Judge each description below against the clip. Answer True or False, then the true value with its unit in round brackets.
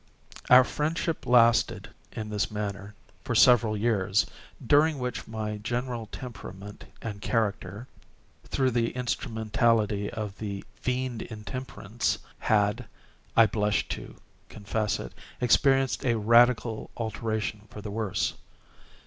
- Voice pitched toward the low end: True (110 Hz)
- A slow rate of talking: True (105 wpm)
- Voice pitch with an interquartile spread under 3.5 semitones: True (2.8 semitones)